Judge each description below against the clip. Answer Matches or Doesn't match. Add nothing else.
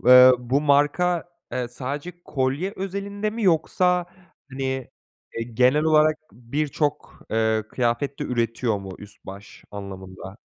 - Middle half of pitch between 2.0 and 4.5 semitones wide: Doesn't match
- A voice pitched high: Doesn't match